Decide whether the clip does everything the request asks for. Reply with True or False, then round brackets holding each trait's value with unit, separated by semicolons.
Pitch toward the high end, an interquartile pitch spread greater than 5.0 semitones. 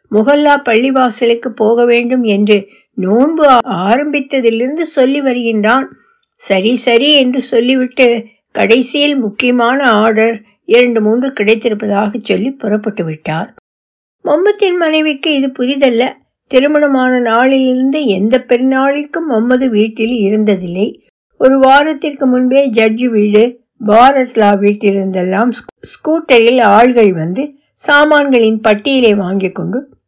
False (245 Hz; 3.7 semitones)